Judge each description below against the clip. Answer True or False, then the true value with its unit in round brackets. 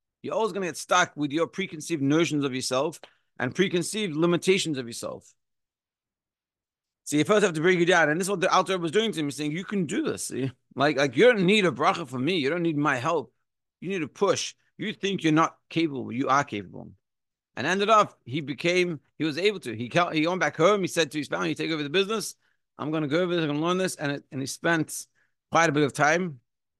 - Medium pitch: True (160 Hz)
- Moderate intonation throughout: True (4.8 semitones)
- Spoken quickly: True (255 wpm)